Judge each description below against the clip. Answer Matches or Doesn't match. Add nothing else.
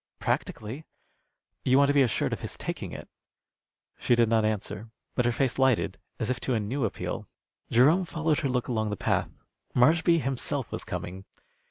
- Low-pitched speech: Matches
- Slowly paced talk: Doesn't match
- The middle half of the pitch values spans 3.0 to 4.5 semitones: Matches